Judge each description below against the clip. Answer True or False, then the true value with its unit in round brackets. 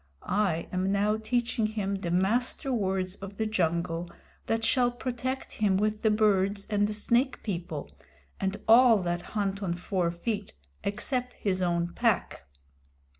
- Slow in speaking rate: False (150 wpm)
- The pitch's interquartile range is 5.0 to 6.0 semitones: False (3.3 semitones)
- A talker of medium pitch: False (200 Hz)